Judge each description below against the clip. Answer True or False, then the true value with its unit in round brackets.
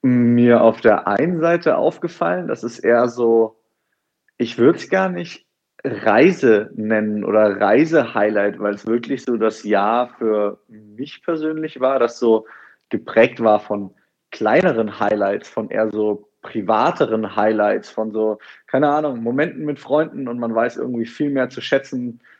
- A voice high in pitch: False (115 Hz)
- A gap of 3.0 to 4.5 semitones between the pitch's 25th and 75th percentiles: True (3.5 semitones)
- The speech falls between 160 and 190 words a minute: False (150 wpm)